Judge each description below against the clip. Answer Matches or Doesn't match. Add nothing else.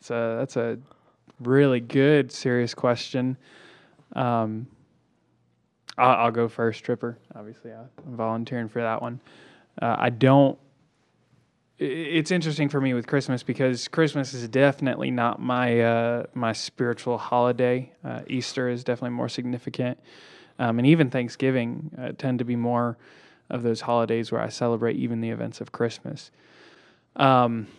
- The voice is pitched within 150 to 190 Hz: Doesn't match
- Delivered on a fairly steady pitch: Matches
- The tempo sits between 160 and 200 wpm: Doesn't match